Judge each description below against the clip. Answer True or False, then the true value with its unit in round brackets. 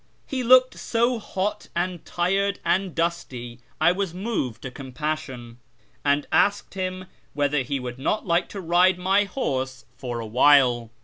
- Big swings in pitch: True (6.7 semitones)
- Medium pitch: True (170 Hz)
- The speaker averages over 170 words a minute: False (160 wpm)